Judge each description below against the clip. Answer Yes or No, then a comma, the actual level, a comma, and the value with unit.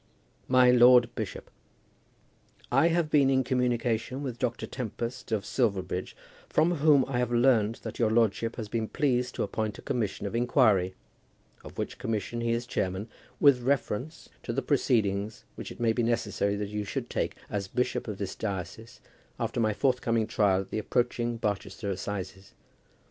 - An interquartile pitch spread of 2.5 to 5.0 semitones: Yes, average, 3.3 semitones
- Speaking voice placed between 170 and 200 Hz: No, low, 115 Hz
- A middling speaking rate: Yes, average, 170 wpm